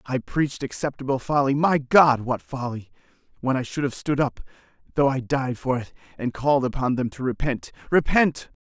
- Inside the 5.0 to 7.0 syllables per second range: Yes, 5.2 syllables/s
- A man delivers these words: Yes, male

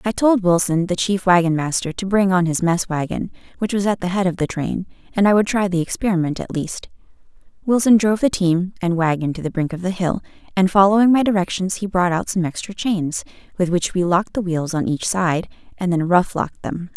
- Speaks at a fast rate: Yes, fast, 230 wpm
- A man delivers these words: No, female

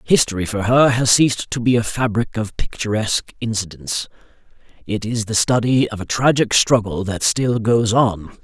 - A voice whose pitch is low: Yes, low, 110 Hz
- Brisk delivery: No, average, 170 wpm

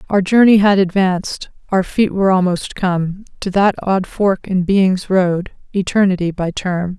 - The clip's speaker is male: No, female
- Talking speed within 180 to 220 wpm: No, average, 165 wpm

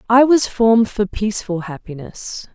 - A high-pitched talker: Yes, high, 215 Hz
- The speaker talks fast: No, average, 140 wpm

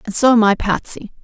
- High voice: Yes, high, 220 Hz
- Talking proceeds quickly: Yes, fast, 245 wpm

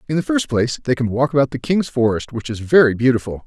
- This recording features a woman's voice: No, male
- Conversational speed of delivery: No, fast, 260 wpm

